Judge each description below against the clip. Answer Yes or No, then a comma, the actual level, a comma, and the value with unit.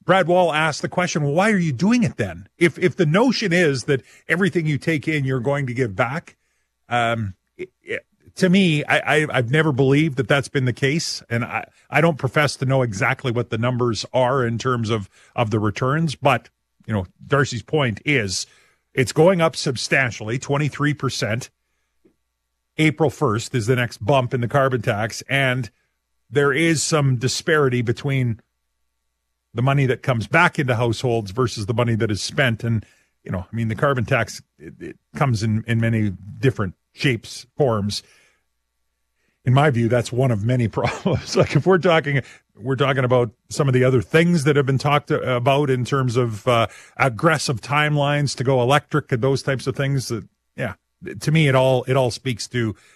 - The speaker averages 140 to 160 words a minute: No, average, 190 wpm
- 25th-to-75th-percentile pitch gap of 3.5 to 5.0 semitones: Yes, average, 4.2 semitones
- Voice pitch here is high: No, low, 130 Hz